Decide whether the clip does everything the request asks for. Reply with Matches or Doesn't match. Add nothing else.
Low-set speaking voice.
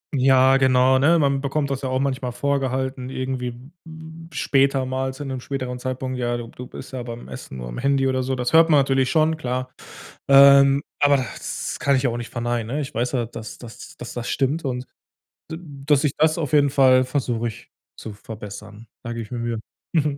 Matches